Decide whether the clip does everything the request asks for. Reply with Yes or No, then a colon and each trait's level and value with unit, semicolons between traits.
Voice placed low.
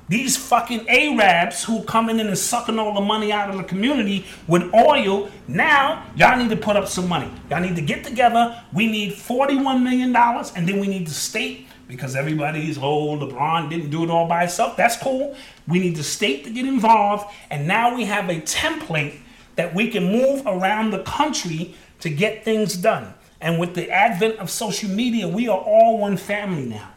No: high, 205 Hz